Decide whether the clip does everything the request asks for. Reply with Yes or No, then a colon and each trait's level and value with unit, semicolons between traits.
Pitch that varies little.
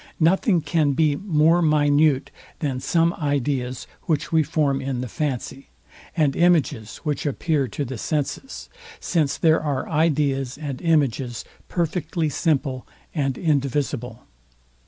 No: average, 3.0 semitones